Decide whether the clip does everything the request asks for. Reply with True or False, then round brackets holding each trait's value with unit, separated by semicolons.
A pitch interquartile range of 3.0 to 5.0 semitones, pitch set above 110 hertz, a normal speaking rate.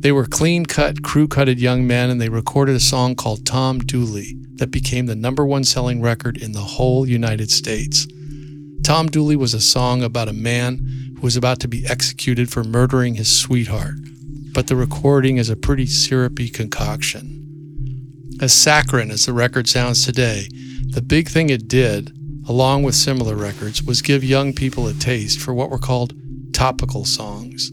False (2.4 semitones; 130 Hz; 175 wpm)